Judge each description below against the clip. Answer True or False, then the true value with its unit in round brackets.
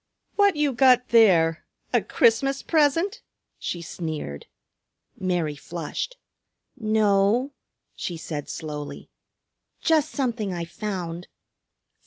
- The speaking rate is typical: False (95 wpm)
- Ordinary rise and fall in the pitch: False (8.3 semitones)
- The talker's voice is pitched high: True (210 Hz)